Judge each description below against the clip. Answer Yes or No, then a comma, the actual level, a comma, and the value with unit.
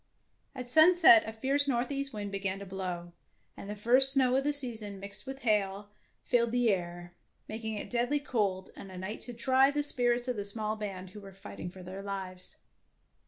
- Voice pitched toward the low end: No, high, 215 Hz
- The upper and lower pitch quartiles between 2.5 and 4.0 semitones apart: No, average, 4.6 semitones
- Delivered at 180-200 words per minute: Yes, average, 195 wpm